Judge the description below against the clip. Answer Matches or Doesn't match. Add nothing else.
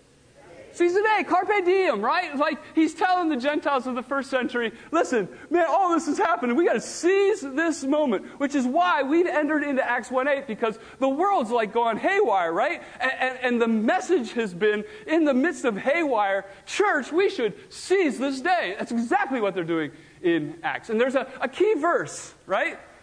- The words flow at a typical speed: Matches